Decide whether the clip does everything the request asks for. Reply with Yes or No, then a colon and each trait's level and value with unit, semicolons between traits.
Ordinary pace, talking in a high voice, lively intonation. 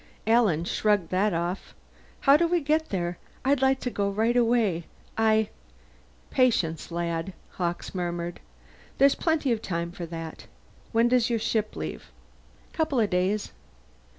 Yes: average, 150 wpm; high, 210 Hz; wide, 6.0 semitones